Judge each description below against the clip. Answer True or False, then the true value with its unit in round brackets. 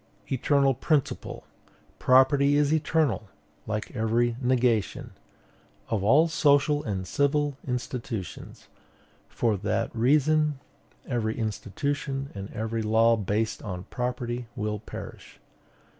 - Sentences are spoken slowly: True (105 wpm)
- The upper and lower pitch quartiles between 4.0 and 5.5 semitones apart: True (4.4 semitones)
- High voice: False (125 Hz)